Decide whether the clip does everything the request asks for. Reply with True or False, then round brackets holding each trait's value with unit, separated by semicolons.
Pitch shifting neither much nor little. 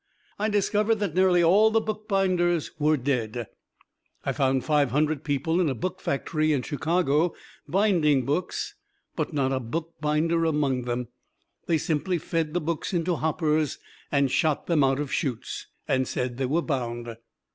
True (4.4 semitones)